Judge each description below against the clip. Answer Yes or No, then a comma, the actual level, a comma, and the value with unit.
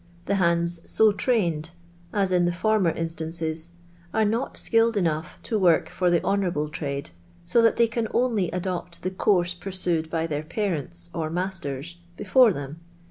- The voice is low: No, medium, 175 Hz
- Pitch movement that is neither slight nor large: Yes, average, 3.8 semitones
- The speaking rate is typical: Yes, average, 160 wpm